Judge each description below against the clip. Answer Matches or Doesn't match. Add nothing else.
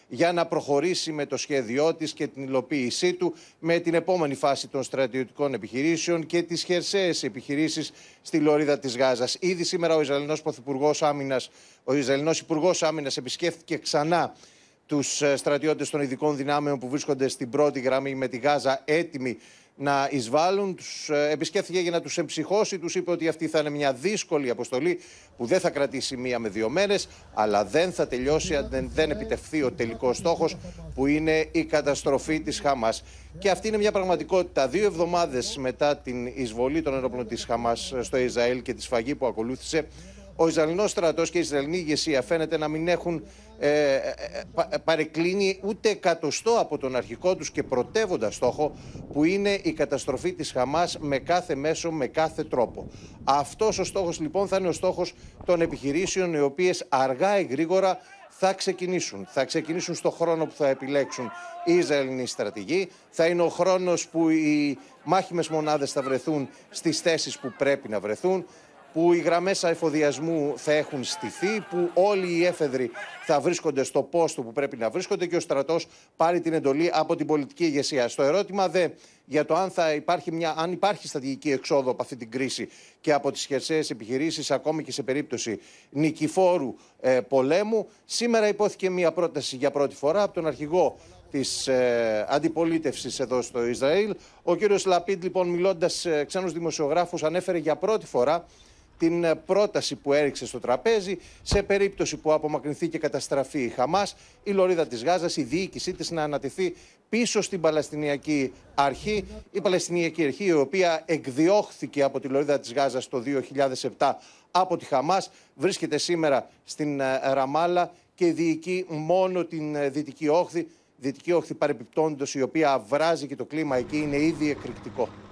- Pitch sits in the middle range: Matches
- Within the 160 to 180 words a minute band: Matches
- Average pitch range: Matches